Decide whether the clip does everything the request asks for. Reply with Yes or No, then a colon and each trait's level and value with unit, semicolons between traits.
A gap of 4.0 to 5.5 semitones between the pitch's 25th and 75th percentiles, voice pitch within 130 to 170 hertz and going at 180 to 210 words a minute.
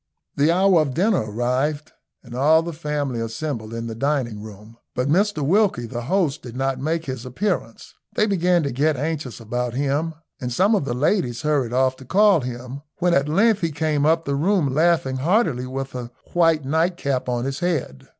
Yes: average, 4.8 semitones; medium, 140 Hz; average, 195 wpm